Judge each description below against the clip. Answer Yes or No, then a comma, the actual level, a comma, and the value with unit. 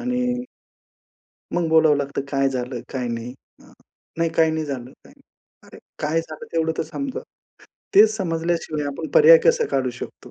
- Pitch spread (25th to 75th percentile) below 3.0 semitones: No, average, 3.9 semitones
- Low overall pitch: No, medium, 160 Hz